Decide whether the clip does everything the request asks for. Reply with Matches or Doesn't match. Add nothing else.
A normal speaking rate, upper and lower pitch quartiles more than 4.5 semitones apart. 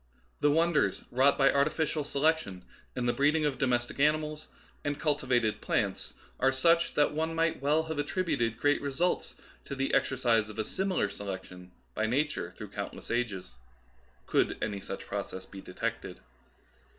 Matches